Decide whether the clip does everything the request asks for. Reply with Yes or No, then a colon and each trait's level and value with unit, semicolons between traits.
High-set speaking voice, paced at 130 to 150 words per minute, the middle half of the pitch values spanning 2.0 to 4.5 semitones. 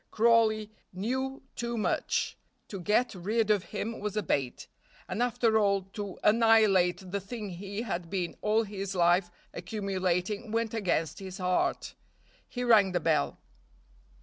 Yes: high, 205 Hz; average, 145 wpm; average, 3.4 semitones